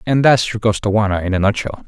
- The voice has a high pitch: No, low, 105 Hz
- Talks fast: Yes, fast, 225 wpm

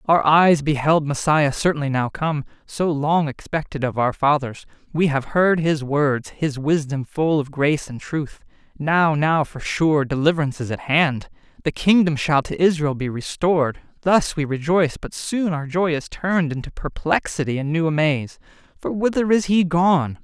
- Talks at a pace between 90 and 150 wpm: No, average, 175 wpm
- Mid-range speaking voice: Yes, medium, 155 Hz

